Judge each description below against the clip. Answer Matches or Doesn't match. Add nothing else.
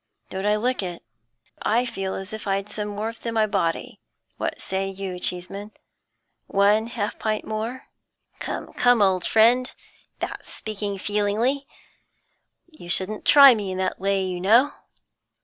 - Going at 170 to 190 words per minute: Doesn't match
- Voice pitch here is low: Doesn't match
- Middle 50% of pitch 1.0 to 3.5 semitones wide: Matches